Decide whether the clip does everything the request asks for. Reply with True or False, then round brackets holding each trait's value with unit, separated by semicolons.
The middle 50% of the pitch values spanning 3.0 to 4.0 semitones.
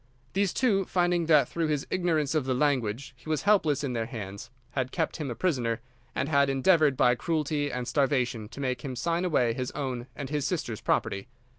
False (4.4 semitones)